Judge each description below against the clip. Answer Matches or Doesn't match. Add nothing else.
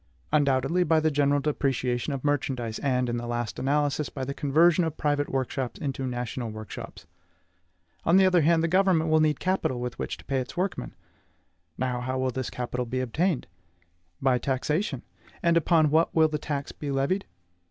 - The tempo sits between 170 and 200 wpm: Matches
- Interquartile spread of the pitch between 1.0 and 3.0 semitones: Doesn't match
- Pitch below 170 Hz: Matches